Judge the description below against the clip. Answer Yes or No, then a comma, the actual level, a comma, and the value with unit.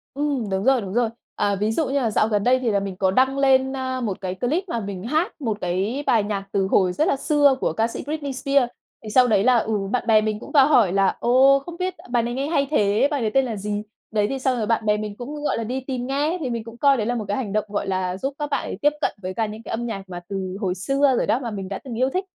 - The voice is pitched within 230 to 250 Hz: Yes, high, 235 Hz